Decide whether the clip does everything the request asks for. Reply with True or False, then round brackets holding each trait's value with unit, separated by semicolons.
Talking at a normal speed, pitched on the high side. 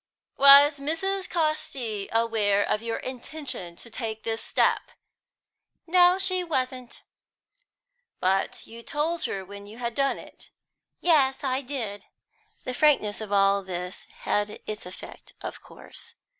False (130 wpm; 245 Hz)